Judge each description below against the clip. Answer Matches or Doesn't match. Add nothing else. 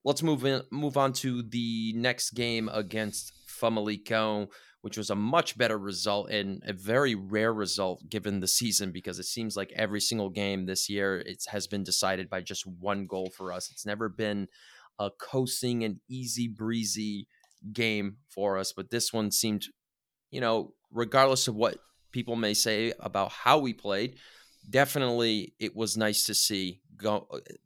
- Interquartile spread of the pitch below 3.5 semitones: Matches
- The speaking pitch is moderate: Doesn't match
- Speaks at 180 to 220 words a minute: Doesn't match